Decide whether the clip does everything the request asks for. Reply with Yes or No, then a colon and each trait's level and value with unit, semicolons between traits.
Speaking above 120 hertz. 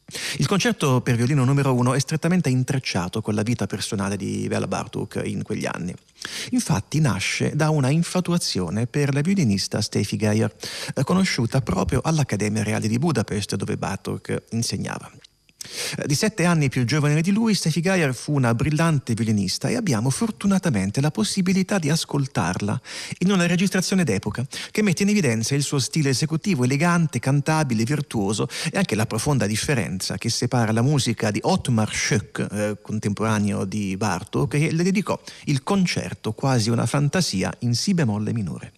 Yes: low, 135 Hz